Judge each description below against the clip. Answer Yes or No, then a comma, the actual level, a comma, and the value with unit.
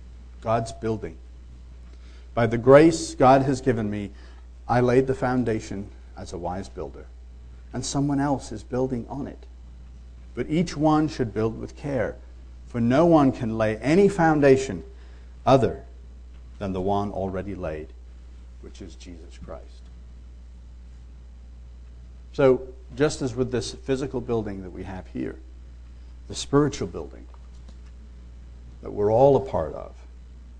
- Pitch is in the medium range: No, very low, 70 Hz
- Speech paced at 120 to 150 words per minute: Yes, slow, 135 wpm